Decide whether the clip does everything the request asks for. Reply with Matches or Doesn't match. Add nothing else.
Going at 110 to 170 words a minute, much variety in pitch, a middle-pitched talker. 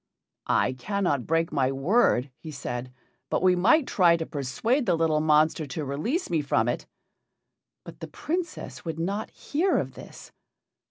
Matches